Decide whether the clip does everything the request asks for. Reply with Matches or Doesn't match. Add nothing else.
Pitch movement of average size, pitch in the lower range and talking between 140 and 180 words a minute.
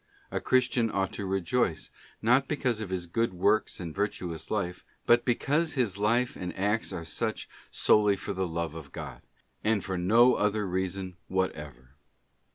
Matches